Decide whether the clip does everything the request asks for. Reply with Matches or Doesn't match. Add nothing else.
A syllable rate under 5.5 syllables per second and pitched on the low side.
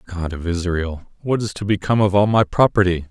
Doesn't match